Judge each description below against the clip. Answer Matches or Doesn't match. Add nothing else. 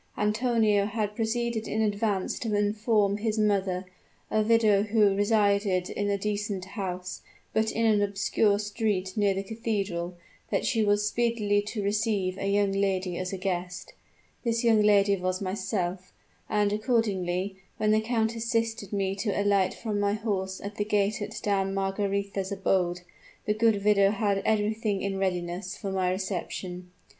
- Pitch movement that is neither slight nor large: Doesn't match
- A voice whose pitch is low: Doesn't match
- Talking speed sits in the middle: Matches